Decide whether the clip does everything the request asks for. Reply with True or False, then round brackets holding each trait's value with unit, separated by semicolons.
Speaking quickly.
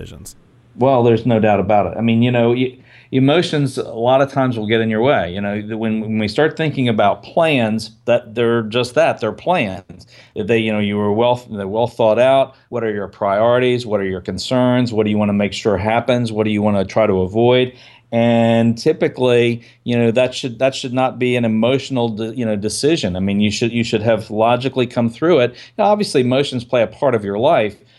True (225 wpm)